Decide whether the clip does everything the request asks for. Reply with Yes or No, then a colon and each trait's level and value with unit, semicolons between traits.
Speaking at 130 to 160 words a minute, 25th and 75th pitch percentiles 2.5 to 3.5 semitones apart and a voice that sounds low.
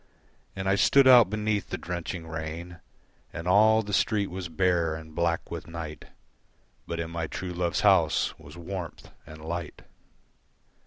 Yes: average, 155 wpm; average, 3.0 semitones; very low, 85 Hz